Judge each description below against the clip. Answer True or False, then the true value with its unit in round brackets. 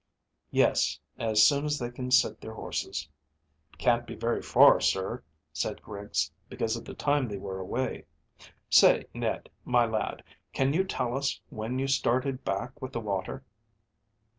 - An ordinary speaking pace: True (160 wpm)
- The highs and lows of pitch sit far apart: False (3.3 semitones)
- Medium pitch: False (120 Hz)